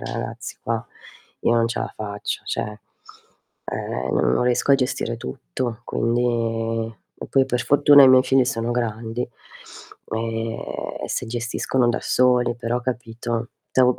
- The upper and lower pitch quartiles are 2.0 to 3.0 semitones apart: No, narrow, 1.6 semitones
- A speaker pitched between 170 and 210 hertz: No, low, 120 Hz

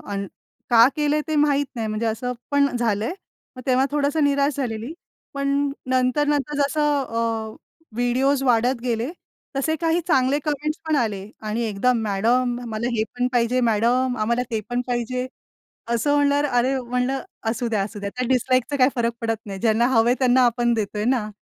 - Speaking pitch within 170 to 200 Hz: No, very high, 250 Hz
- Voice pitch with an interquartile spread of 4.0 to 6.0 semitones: No, average, 3.4 semitones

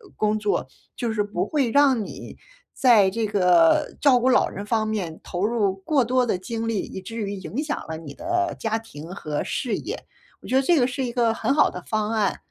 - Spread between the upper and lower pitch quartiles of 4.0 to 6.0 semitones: Yes, average, 4.4 semitones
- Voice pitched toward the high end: Yes, high, 225 Hz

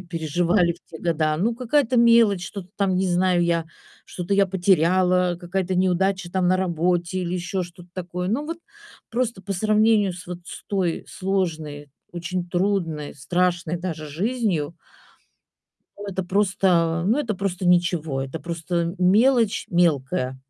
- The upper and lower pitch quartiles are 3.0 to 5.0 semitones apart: No, narrow, 2.4 semitones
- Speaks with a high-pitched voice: No, medium, 180 Hz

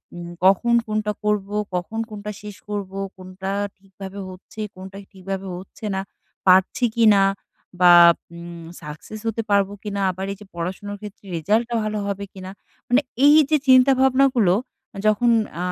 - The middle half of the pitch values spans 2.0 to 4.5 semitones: Yes, narrow, 2.4 semitones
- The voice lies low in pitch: No, high, 200 Hz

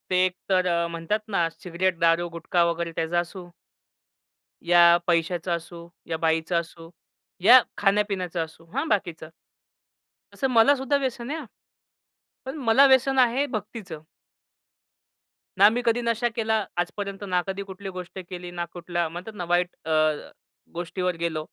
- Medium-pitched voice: Yes, medium, 180 Hz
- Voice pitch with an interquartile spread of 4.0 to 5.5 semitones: Yes, average, 4.5 semitones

